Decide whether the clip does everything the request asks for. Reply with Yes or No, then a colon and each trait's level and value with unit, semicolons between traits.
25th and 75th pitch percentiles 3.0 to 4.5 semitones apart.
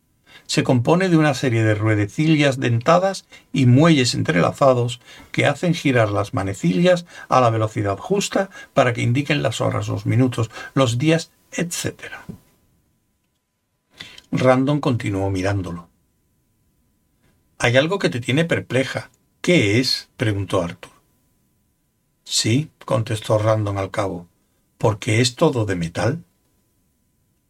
No: wide, 5.4 semitones